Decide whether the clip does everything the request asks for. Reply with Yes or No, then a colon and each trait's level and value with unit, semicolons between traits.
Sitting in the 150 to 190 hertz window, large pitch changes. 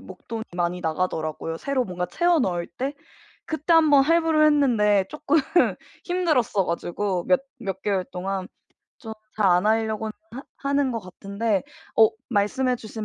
No: high, 220 Hz; wide, 6.9 semitones